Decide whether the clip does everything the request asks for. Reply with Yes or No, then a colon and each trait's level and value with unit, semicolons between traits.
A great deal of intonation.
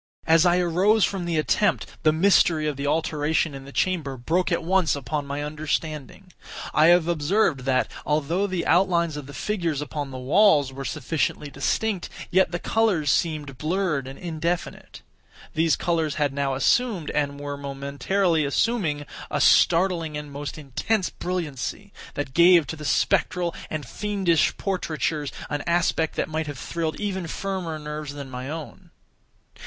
No: average, 3.6 semitones